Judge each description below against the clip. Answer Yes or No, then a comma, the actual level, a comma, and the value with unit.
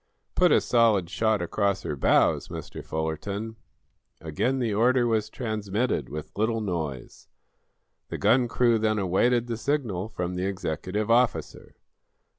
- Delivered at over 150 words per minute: No, slow, 135 wpm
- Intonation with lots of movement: No, average, 4.3 semitones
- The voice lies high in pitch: No, low, 105 Hz